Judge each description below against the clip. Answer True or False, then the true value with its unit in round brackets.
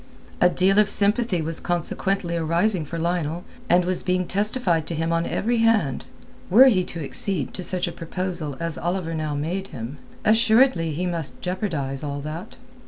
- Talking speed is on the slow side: False (170 wpm)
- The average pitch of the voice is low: False (175 Hz)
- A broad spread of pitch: False (3.3 semitones)